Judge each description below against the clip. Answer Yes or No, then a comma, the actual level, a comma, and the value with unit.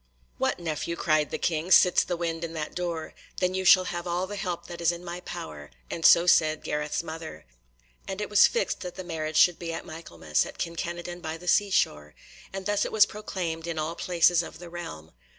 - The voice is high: No, medium, 170 Hz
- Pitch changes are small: Yes, narrow, 2.0 semitones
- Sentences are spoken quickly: Yes, fast, 220 wpm